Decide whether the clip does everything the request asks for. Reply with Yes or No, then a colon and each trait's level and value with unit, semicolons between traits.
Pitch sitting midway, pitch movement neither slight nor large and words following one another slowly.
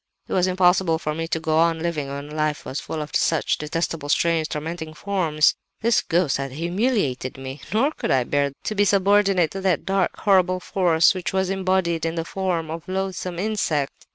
No: medium, 170 Hz; average, 3.7 semitones; average, 190 wpm